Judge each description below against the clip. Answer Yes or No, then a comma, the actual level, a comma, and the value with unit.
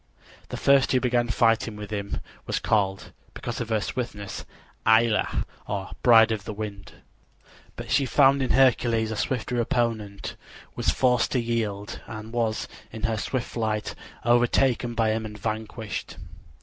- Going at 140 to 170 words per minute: Yes, average, 150 wpm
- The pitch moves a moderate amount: No, narrow, 2.1 semitones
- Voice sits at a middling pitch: No, low, 115 Hz